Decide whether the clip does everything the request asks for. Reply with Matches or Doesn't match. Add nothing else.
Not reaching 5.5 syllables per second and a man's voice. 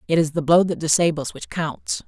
Doesn't match